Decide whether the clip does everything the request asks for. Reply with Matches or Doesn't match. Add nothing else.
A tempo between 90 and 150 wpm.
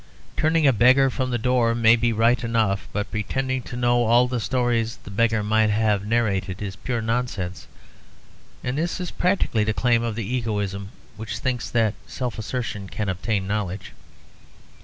Doesn't match